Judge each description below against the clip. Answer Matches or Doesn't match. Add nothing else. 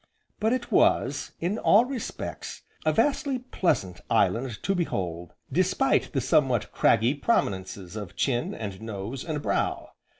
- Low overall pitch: Matches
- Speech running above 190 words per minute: Doesn't match